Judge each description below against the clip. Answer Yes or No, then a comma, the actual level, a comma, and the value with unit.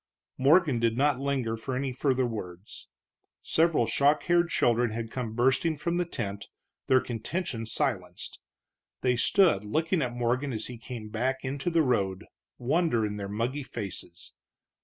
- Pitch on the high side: No, low, 125 Hz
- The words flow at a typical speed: Yes, average, 155 wpm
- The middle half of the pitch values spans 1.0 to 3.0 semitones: No, average, 4.2 semitones